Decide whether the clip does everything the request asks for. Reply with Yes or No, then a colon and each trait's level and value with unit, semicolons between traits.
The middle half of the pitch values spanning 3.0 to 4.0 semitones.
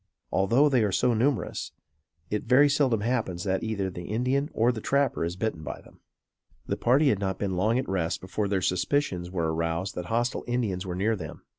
No: average, 5.1 semitones